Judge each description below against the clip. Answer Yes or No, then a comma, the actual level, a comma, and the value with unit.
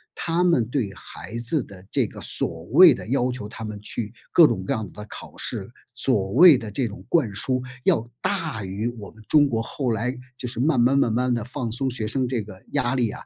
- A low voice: Yes, low, 120 Hz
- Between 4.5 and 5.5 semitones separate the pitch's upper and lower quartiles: No, average, 3.8 semitones